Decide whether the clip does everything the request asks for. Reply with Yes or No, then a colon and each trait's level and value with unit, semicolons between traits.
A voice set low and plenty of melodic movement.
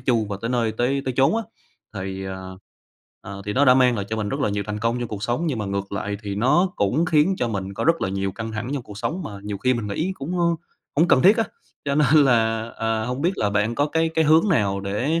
Yes: low, 115 Hz; wide, 5.9 semitones